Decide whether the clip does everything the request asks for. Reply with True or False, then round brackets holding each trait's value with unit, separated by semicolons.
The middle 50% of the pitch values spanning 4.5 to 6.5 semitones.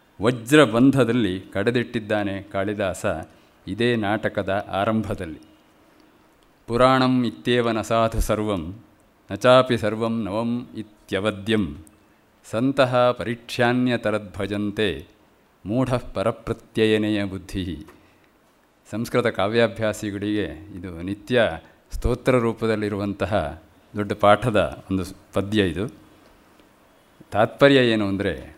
False (2.9 semitones)